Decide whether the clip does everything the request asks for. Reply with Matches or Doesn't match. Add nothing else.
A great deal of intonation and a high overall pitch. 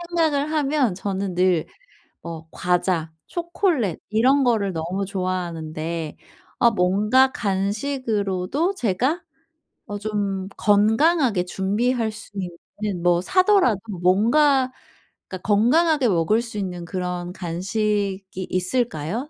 Matches